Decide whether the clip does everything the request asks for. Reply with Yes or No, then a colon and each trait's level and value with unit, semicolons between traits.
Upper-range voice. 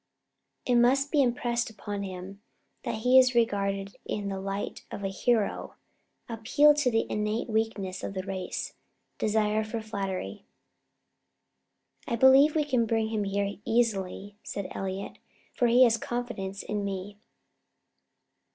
Yes: high, 215 Hz